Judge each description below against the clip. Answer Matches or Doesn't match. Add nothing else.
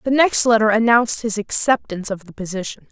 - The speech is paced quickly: Doesn't match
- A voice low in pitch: Doesn't match